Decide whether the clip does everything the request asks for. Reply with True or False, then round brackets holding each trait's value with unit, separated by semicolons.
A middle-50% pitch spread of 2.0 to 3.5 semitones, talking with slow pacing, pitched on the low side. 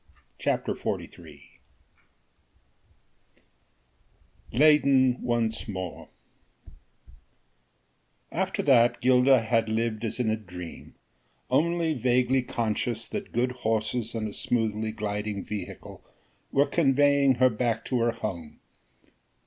True (2.9 semitones; 100 wpm; 115 Hz)